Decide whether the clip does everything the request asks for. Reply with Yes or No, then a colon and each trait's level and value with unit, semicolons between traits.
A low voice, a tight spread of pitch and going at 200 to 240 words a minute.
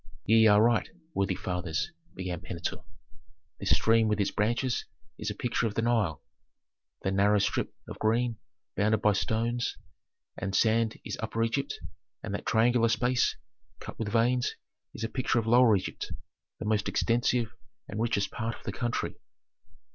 No: low, 110 Hz; narrow, 2.3 semitones; average, 160 wpm